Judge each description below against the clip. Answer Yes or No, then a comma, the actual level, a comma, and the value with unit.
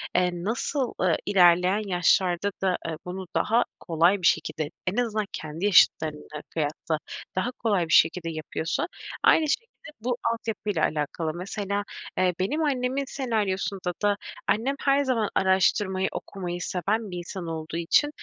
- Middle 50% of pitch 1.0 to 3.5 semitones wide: No, average, 4.2 semitones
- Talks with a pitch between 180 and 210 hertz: Yes, high, 190 Hz